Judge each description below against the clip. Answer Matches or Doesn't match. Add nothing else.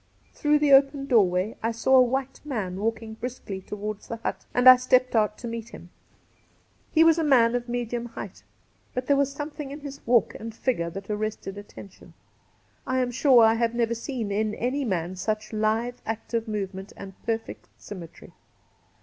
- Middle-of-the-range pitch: Doesn't match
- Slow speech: Doesn't match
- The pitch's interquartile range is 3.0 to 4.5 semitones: Matches